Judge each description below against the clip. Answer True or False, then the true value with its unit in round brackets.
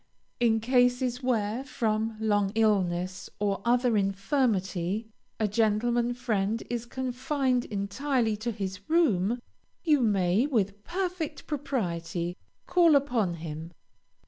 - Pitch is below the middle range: False (225 Hz)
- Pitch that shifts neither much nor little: True (4.3 semitones)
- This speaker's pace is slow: True (110 wpm)